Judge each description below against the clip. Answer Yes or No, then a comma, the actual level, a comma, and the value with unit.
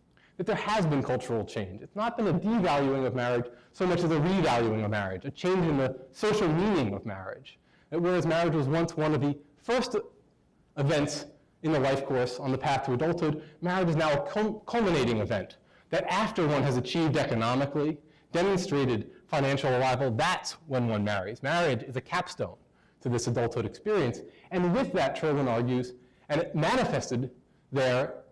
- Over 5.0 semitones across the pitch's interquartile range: Yes, wide, 5.5 semitones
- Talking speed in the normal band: Yes, average, 180 wpm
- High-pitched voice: No, medium, 145 Hz